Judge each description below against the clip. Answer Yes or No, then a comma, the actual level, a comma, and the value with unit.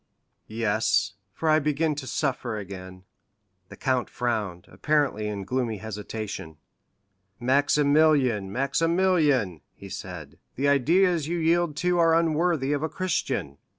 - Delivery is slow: Yes, slow, 120 wpm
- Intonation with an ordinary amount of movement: No, wide, 7.0 semitones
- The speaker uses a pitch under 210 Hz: Yes, low, 135 Hz